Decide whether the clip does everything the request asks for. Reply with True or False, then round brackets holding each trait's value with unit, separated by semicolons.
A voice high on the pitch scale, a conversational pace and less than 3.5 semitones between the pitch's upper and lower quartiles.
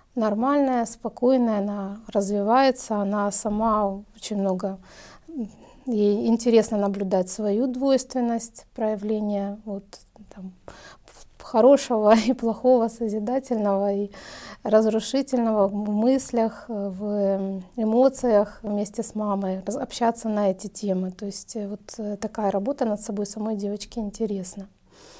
False (215 Hz; 100 wpm; 2.4 semitones)